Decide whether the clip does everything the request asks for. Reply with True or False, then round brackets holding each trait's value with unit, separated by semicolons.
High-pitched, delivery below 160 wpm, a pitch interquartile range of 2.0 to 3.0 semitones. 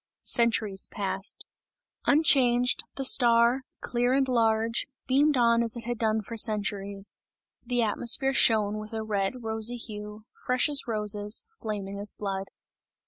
True (225 Hz; 140 wpm; 2.7 semitones)